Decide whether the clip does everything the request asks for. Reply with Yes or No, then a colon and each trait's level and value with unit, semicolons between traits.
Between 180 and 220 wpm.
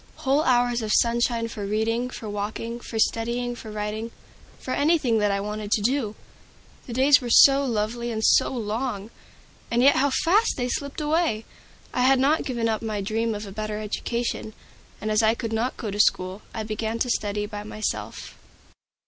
Yes: average, 185 wpm